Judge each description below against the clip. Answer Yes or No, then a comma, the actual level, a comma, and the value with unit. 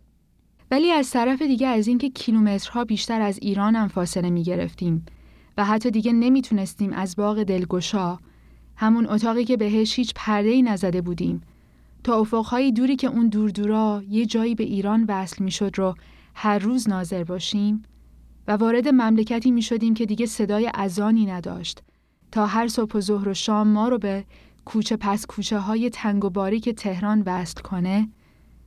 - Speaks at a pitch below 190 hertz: No, high, 215 Hz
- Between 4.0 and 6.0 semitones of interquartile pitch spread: No, average, 2.8 semitones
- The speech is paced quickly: Yes, fast, 165 wpm